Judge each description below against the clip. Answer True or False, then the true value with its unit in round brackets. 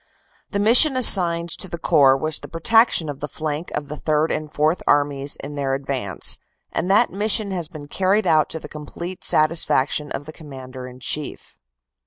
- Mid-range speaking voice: True (155 Hz)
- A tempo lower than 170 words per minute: False (190 wpm)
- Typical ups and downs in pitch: True (3.9 semitones)